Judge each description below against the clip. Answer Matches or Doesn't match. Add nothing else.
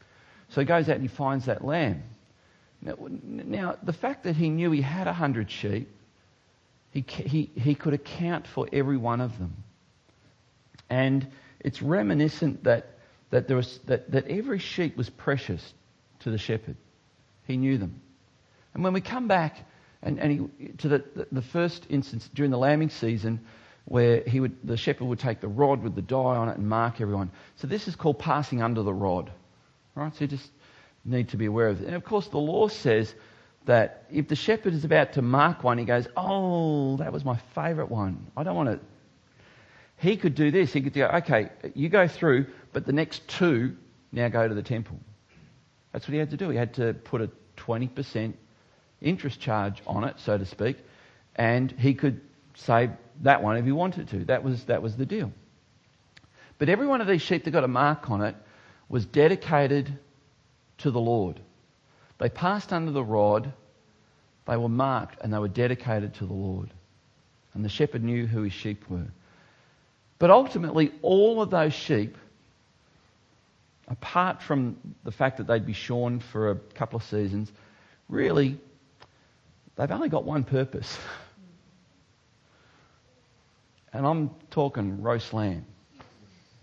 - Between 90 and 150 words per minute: Doesn't match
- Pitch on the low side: Matches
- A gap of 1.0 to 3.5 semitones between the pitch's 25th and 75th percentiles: Doesn't match